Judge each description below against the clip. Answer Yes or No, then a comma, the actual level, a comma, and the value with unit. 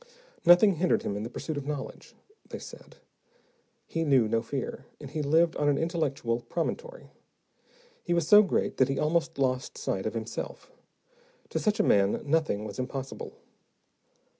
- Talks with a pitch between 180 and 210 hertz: No, medium, 145 Hz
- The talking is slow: No, average, 165 wpm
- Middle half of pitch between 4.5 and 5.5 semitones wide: Yes, average, 4.8 semitones